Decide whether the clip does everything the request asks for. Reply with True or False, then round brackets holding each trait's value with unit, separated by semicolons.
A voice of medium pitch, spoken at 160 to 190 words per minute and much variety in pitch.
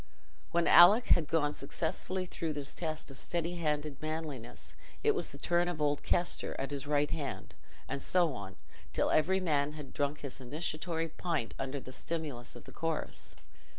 False (155 Hz; 170 wpm; 3.1 semitones)